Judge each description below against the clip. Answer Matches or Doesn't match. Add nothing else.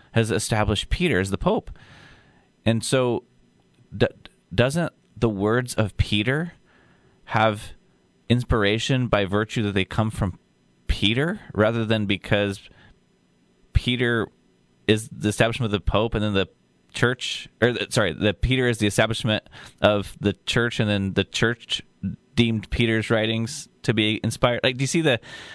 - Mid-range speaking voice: Doesn't match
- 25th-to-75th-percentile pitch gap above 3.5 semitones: Doesn't match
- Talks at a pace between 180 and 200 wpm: Doesn't match